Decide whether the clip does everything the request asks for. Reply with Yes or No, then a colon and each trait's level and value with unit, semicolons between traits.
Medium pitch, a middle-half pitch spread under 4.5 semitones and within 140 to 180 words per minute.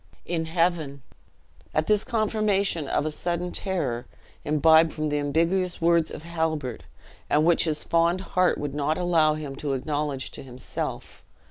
Yes: medium, 160 Hz; average, 2.9 semitones; average, 150 wpm